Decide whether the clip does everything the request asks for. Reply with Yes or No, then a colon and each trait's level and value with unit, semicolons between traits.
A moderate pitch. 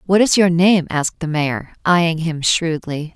Yes: medium, 165 Hz